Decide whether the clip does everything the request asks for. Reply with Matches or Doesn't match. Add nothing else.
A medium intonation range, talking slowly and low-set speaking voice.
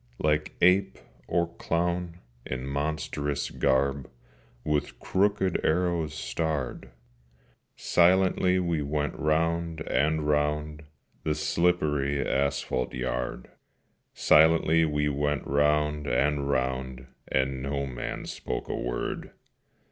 Matches